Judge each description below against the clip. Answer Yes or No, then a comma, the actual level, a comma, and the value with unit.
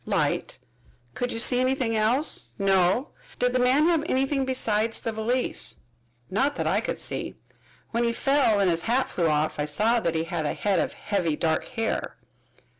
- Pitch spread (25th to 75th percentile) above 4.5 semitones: Yes, wide, 5.6 semitones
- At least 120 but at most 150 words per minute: No, average, 185 wpm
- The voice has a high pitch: Yes, high, 225 Hz